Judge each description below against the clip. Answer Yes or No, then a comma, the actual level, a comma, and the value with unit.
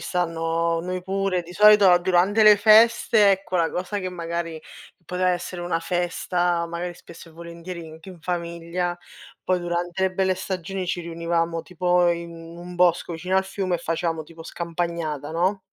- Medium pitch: Yes, medium, 175 Hz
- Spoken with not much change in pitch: Yes, narrow, 1.7 semitones